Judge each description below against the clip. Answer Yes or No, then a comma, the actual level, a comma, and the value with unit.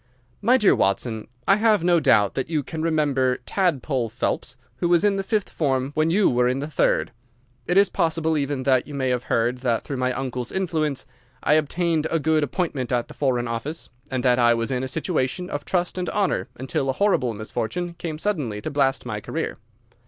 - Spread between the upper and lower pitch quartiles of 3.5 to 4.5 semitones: No, average, 5.2 semitones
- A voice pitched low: No, medium, 145 Hz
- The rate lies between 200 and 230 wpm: Yes, fast, 205 wpm